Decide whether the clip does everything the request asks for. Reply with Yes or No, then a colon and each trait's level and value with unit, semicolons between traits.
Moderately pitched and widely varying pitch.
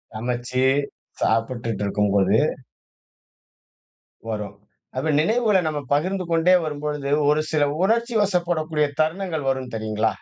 Yes: medium, 150 Hz; wide, 7.4 semitones